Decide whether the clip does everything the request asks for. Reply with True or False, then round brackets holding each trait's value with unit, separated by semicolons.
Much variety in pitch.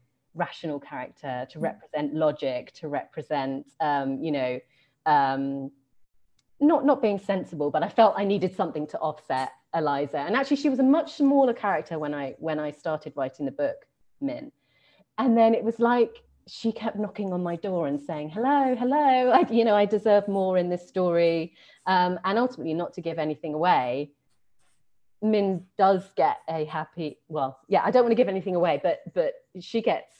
True (7.1 semitones)